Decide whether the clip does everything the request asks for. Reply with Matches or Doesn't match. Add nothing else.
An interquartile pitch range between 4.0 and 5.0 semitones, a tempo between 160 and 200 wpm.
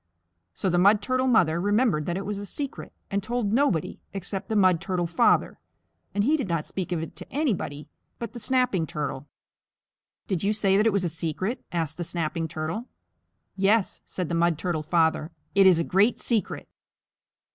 Matches